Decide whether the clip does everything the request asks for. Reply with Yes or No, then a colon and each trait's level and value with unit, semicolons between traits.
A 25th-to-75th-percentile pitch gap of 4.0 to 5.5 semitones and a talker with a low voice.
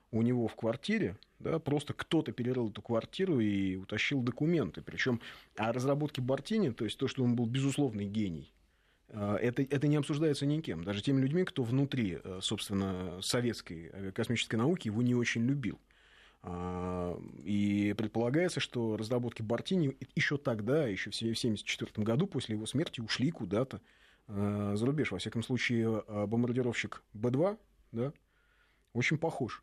Yes: average, 4.7 semitones; low, 120 Hz